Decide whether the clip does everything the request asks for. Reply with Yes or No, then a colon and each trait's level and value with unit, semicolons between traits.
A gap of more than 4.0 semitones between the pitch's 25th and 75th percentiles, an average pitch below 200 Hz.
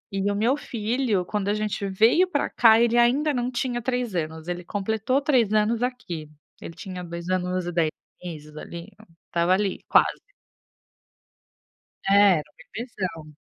No: wide, 5.4 semitones; high, 205 Hz